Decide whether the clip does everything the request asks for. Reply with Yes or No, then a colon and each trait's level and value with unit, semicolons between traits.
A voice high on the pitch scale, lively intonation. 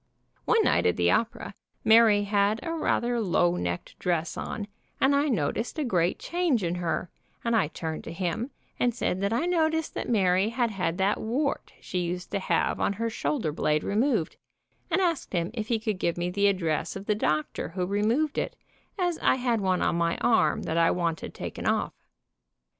Yes: high, 205 Hz; wide, 5.7 semitones